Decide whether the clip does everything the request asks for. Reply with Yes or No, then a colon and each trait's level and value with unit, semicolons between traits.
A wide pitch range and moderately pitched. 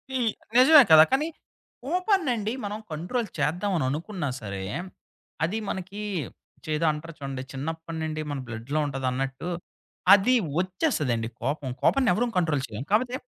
Yes: wide, 8.0 semitones; medium, 165 Hz